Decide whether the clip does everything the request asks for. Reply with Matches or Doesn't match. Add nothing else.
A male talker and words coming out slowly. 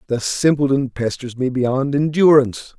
Matches